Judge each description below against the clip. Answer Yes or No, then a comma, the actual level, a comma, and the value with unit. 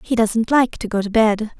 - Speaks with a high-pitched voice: Yes, high, 220 Hz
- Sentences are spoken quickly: Yes, fast, 265 wpm